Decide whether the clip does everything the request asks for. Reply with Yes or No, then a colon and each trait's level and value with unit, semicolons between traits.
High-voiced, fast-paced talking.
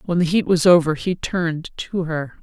No: medium, 170 Hz; fast, 225 wpm